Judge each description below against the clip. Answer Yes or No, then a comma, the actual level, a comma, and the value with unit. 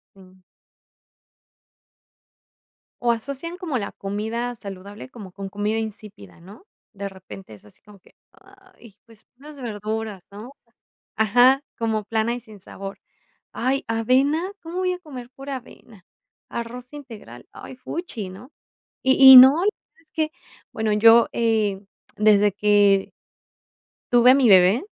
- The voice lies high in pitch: Yes, high, 225 Hz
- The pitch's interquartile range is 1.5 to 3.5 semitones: No, average, 4.3 semitones